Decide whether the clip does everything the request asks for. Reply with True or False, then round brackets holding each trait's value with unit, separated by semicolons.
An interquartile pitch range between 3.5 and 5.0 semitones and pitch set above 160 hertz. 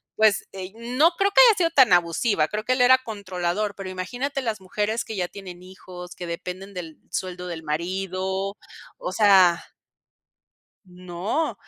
True (3.8 semitones; 190 Hz)